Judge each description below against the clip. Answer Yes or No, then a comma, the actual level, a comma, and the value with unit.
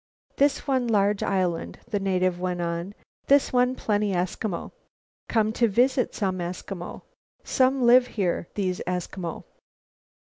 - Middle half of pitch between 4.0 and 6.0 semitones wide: Yes, average, 5.1 semitones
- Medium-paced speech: No, slow, 130 wpm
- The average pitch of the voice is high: Yes, high, 200 Hz